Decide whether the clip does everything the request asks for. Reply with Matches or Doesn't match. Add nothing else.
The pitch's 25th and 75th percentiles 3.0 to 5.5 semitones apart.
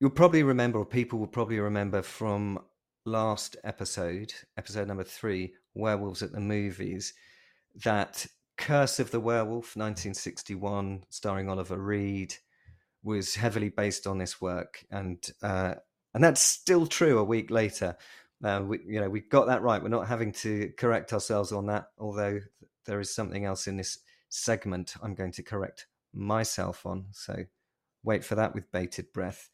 Doesn't match